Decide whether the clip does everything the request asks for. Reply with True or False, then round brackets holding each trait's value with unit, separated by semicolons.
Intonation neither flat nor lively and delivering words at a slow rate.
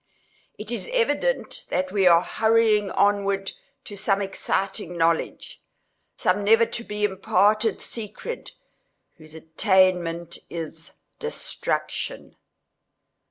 True (3.6 semitones; 95 wpm)